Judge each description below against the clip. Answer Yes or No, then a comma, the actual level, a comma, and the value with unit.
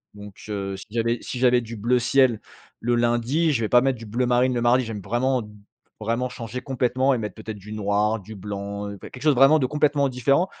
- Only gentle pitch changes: No, average, 3.3 semitones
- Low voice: Yes, low, 120 Hz